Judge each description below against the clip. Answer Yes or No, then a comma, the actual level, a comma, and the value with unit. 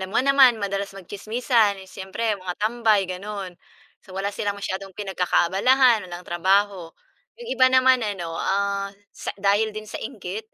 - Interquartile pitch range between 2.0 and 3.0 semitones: Yes, narrow, 2.6 semitones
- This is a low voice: No, high, 200 Hz